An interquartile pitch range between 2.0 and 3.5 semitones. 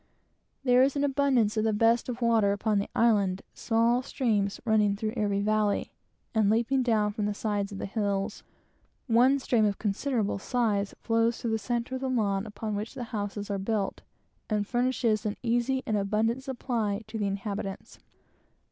Yes: average, 2.8 semitones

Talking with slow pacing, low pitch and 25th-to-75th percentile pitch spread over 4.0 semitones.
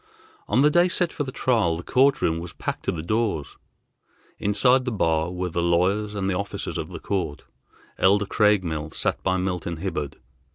No: average, 190 wpm; very low, 95 Hz; average, 4.5 semitones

